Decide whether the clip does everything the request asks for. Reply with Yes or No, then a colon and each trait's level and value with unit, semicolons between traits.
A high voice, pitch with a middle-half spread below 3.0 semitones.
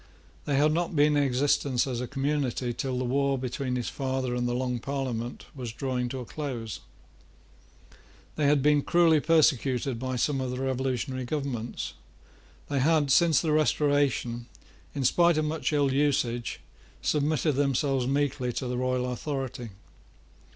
No: low, 135 Hz; narrow, 2.6 semitones